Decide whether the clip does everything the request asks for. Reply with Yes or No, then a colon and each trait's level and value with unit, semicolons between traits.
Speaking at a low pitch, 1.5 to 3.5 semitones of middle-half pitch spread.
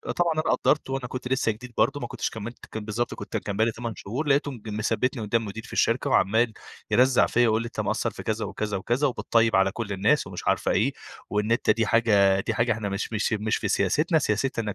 Yes: low, 115 Hz; average, 2.9 semitones